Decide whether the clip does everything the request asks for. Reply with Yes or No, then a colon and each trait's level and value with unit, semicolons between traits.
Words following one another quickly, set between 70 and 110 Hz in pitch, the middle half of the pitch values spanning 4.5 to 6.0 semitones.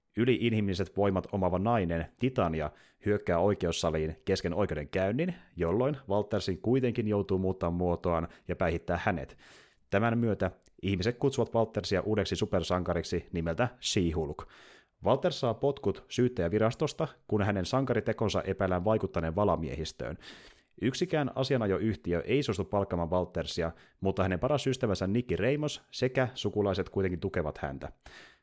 No: average, 120 wpm; low, 100 Hz; average, 5.0 semitones